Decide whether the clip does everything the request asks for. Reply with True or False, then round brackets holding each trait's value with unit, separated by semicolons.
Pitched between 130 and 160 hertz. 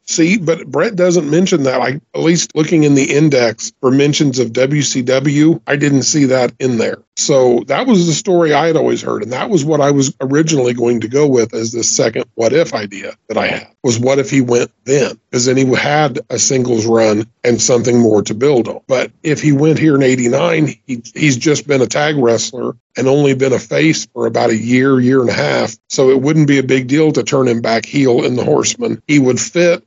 True (135 Hz)